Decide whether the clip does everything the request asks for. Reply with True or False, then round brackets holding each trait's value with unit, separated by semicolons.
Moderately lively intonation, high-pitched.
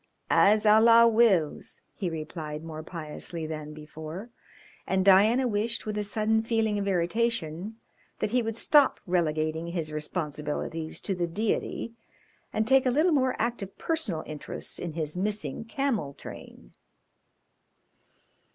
False (6.1 semitones; 195 Hz)